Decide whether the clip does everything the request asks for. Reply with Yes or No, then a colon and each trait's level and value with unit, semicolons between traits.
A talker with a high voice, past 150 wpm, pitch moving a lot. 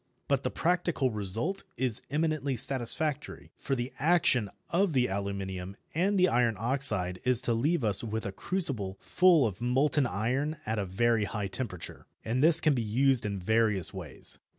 No: low, 120 Hz; average, 165 wpm; wide, 6.1 semitones